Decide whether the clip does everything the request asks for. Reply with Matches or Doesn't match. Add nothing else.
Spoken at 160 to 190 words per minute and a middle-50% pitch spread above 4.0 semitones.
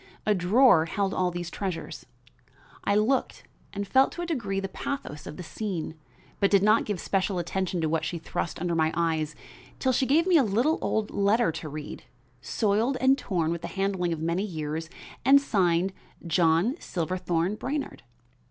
Matches